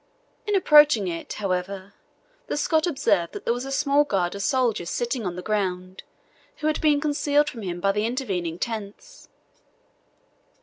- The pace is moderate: Yes, average, 160 wpm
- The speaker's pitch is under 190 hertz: No, high, 220 Hz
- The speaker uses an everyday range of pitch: No, wide, 7.5 semitones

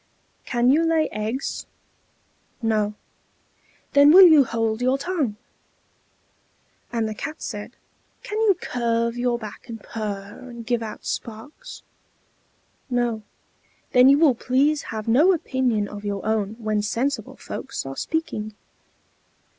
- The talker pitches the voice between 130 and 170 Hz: No, high, 240 Hz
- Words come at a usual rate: No, slow, 130 wpm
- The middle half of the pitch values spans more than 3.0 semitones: Yes, average, 4.3 semitones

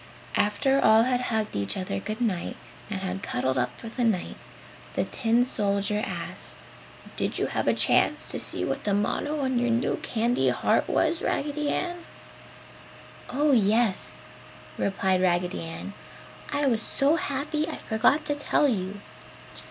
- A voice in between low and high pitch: No, high, 225 Hz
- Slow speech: No, average, 155 wpm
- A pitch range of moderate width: No, wide, 5.8 semitones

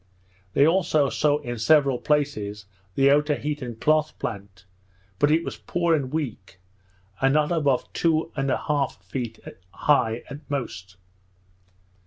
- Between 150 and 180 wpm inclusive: No, slow, 135 wpm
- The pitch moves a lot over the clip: No, average, 4.6 semitones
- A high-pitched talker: No, medium, 140 Hz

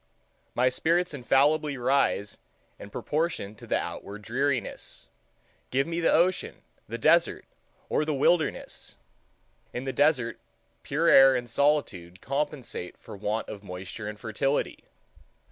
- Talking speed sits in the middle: No, slow, 130 wpm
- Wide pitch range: Yes, wide, 5.8 semitones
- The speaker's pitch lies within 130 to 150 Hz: Yes, low, 135 Hz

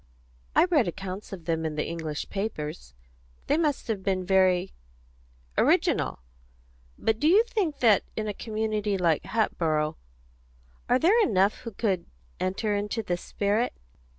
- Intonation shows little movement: No, average, 4.3 semitones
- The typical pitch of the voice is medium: No, high, 200 Hz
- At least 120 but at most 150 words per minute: Yes, average, 145 wpm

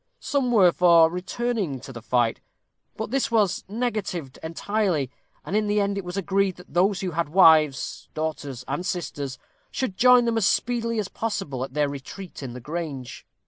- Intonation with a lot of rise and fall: Yes, wide, 6.3 semitones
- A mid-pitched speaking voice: Yes, medium, 180 Hz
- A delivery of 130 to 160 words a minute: No, average, 180 wpm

